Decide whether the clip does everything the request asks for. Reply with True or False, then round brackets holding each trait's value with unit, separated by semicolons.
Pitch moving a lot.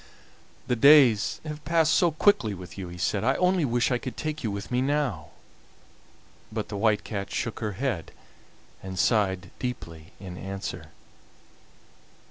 True (6.4 semitones)